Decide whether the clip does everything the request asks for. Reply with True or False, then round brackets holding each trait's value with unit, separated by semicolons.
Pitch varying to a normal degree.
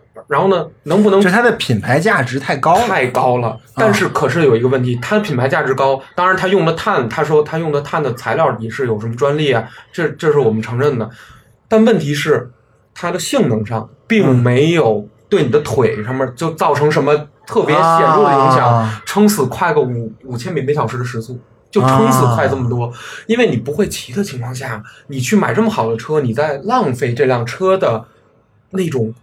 False (5.9 semitones)